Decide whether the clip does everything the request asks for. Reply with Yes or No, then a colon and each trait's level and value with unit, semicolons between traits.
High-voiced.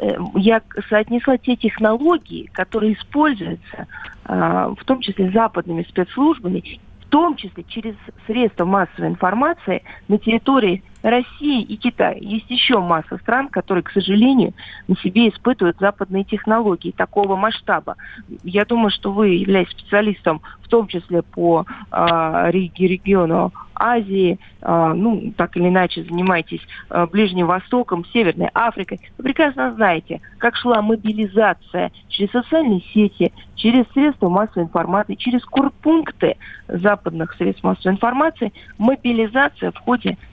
Yes: high, 210 Hz